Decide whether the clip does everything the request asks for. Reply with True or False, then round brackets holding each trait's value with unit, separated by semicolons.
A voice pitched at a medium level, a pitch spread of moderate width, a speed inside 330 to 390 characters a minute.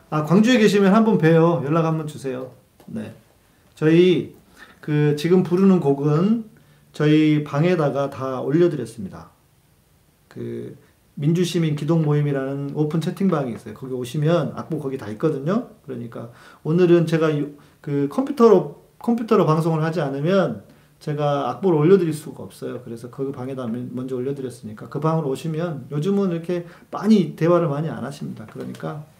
True (155 Hz; 4.3 semitones; 335 characters per minute)